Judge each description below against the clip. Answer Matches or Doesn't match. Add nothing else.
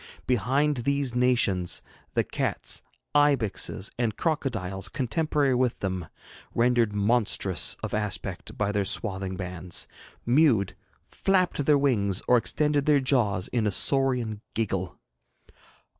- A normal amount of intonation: Doesn't match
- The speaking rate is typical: Doesn't match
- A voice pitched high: Doesn't match